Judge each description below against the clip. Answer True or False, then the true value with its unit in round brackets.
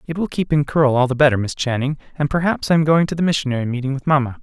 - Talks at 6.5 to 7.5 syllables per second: True (7.1 syllables/s)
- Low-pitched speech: False (145 Hz)